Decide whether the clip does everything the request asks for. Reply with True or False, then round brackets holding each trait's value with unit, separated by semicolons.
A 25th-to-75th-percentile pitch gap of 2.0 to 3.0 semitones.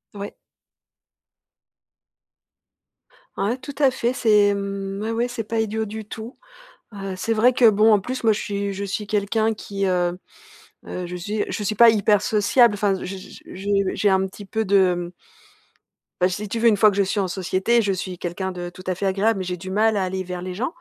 True (2.6 semitones)